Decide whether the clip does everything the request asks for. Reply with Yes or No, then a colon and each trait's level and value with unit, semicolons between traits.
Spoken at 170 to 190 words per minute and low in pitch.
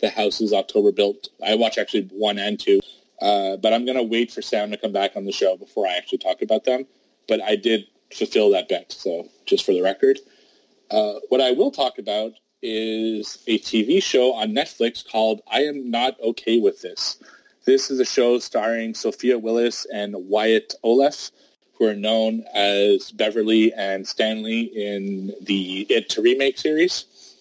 Yes: average, 185 wpm; low, 115 Hz